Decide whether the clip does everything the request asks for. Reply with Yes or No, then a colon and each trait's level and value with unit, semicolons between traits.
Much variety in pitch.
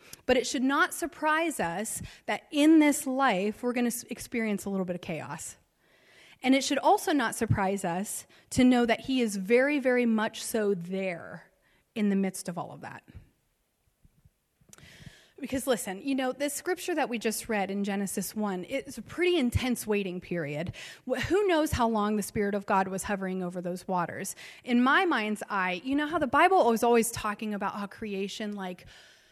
Yes: wide, 5.7 semitones